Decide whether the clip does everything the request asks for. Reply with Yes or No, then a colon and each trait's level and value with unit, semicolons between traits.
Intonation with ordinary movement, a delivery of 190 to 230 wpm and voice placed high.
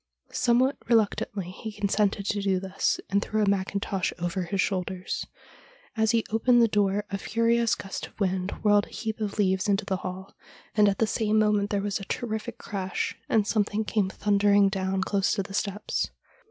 No: narrow, 1.9 semitones; average, 195 wpm; high, 205 Hz